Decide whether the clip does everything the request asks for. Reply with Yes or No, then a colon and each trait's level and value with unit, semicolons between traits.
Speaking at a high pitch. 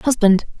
Yes: high, 220 Hz